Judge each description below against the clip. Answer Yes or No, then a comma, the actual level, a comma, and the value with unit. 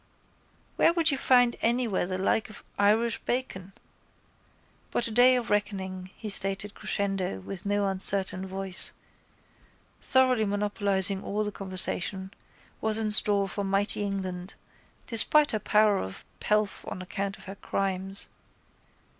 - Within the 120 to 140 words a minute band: Yes, slow, 135 wpm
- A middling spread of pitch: No, narrow, 2.1 semitones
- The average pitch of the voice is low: No, high, 200 Hz